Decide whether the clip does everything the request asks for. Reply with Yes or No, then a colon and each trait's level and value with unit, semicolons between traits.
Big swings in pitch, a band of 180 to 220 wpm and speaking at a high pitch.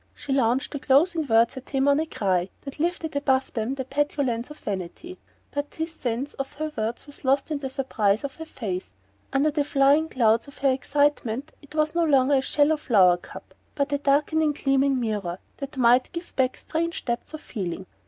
No: average, 3.8 semitones; average, 200 wpm; very high, 275 Hz